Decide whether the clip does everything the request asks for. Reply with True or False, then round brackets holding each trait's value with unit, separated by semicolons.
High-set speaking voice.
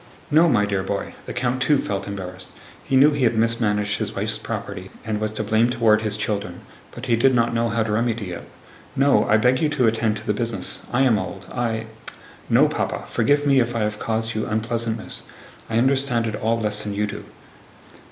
False (115 Hz)